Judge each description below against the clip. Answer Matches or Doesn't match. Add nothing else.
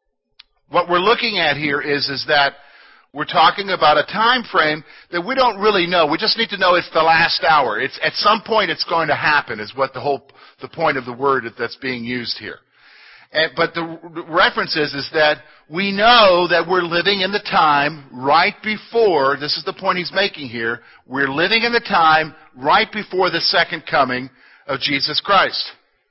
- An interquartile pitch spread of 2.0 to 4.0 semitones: Doesn't match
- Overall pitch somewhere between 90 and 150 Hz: Doesn't match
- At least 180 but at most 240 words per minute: Matches